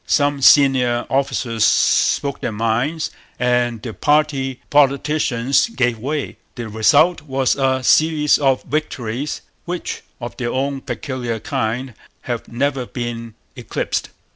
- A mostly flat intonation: No, average, 3.2 semitones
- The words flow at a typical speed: No, slow, 120 wpm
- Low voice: Yes, low, 130 Hz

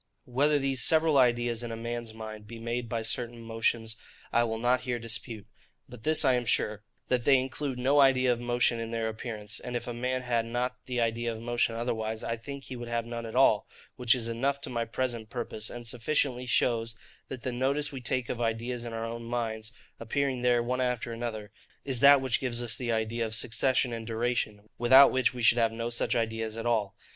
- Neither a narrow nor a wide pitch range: No, narrow, 1.8 semitones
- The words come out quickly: Yes, fast, 220 wpm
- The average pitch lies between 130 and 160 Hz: No, low, 120 Hz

